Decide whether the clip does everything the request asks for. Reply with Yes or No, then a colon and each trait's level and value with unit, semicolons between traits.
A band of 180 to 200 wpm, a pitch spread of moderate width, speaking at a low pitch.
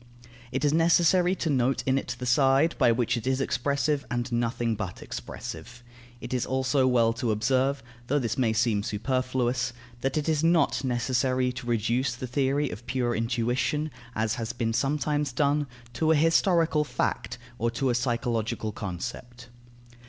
No: average, 165 wpm; average, 3.0 semitones; low, 125 Hz